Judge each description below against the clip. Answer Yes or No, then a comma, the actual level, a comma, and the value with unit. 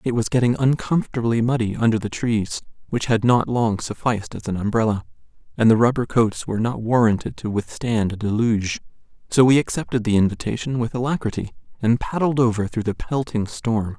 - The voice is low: Yes, low, 115 Hz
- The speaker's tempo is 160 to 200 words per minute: Yes, average, 175 wpm